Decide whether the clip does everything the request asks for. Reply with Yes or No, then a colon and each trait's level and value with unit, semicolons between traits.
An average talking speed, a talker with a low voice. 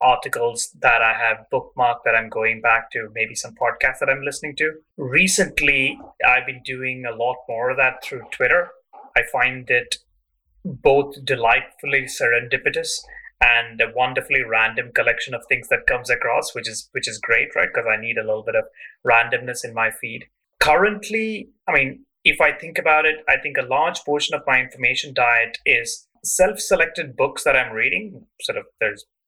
No: average, 180 wpm; medium, 155 Hz